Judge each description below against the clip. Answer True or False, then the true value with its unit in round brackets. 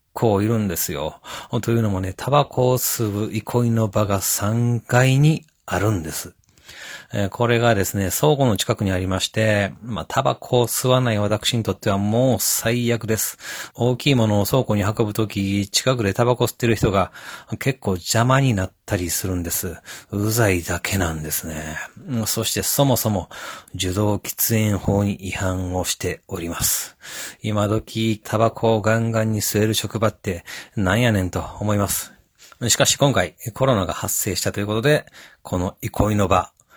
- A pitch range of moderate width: True (3.5 semitones)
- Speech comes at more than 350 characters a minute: False (320 characters per minute)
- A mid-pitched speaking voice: False (110 Hz)